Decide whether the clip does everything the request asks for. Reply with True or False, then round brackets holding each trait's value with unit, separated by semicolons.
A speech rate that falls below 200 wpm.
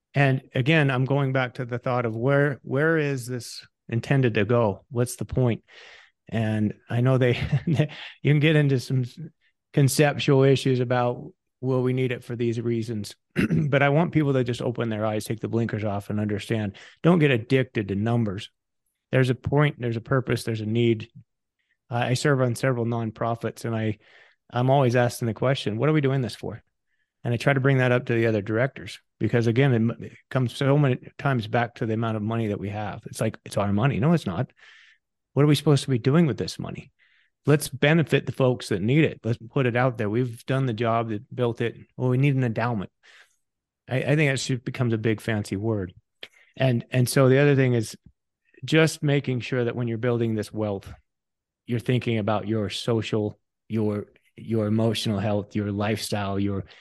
False (205 wpm)